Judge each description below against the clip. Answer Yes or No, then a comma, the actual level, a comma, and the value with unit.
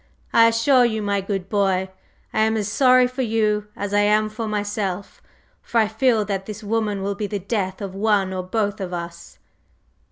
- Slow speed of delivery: No, average, 195 wpm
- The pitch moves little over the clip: Yes, narrow, 2.1 semitones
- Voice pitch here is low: No, high, 210 Hz